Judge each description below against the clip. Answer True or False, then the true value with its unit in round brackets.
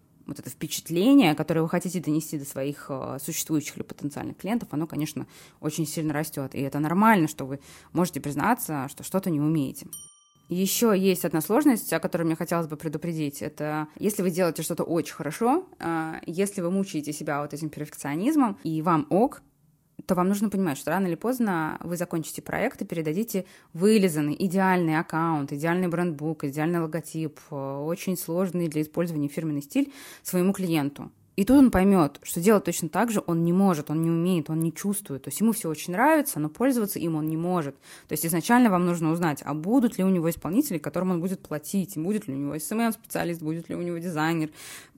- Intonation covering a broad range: False (3.8 semitones)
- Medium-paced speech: False (190 wpm)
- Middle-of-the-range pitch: True (170 Hz)